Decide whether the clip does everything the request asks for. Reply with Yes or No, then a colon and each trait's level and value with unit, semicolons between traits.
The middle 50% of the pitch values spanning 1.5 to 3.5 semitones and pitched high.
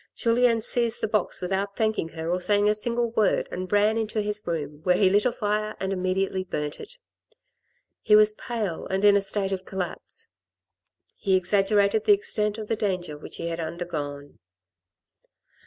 Yes: average, 2.9 semitones; high, 200 Hz